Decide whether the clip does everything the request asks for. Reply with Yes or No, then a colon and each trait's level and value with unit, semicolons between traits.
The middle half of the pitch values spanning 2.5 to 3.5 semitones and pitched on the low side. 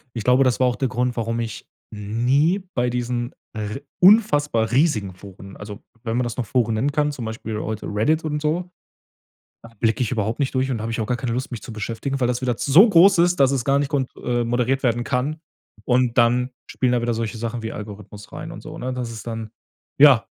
Yes: average, 3.2 semitones; low, 120 Hz